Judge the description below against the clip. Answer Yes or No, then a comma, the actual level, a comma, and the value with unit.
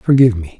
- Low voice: Yes, low, 110 Hz